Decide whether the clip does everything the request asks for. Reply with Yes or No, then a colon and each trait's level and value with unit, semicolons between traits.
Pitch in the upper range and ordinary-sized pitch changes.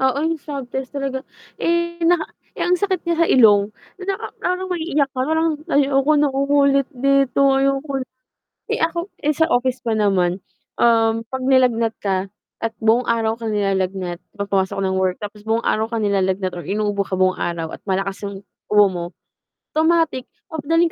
No: very high, 250 Hz; wide, 6.4 semitones